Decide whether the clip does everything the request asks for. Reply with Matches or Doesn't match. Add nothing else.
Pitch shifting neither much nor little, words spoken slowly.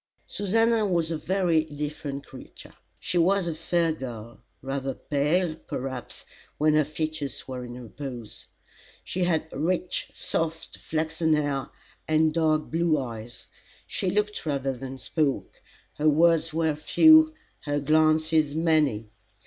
Matches